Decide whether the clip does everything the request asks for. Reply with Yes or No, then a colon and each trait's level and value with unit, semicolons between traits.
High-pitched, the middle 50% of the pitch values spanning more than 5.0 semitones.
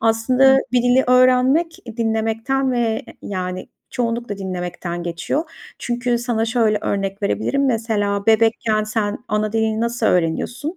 No: high, 225 Hz; average, 3.1 semitones